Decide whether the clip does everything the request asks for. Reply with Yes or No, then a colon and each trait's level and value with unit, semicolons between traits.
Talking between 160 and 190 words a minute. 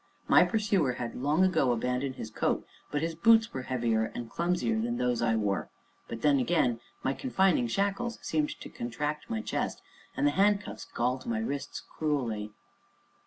Yes: average, 165 wpm